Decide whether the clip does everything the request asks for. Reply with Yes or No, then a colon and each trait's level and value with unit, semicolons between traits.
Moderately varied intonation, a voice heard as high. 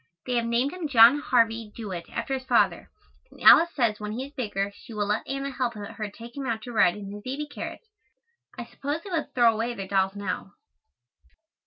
Yes: average, 4.2 semitones; high, 235 Hz